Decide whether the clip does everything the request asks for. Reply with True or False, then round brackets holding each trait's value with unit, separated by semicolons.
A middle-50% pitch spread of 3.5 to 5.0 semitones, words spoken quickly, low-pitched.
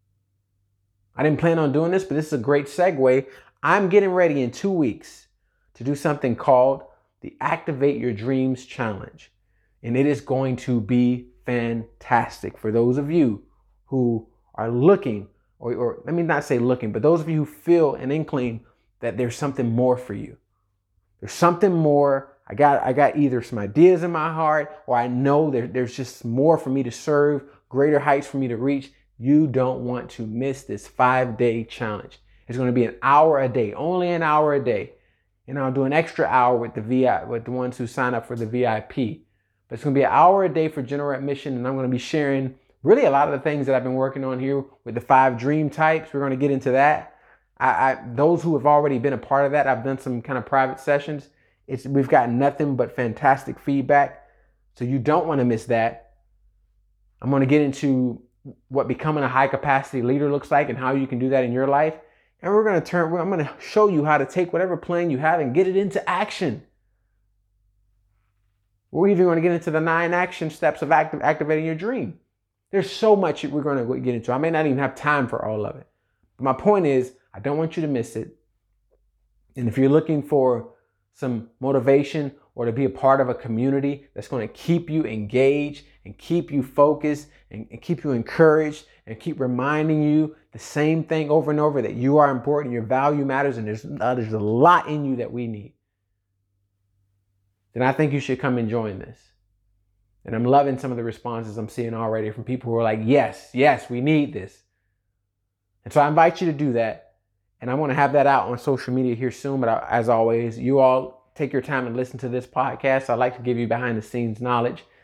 True (4.1 semitones; 220 wpm; 130 Hz)